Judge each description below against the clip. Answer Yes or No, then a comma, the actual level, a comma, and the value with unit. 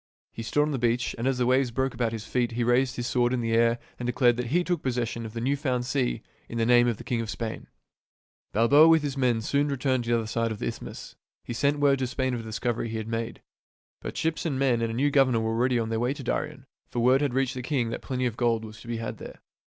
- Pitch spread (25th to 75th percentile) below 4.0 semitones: Yes, narrow, 2.5 semitones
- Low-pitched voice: Yes, low, 120 Hz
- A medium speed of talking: No, fast, 280 wpm